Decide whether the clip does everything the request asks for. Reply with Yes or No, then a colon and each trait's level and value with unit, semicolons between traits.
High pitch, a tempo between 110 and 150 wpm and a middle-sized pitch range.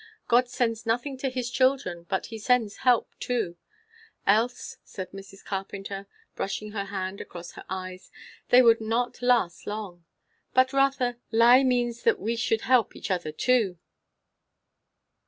Yes: high, 225 Hz; average, 145 wpm; average, 4.2 semitones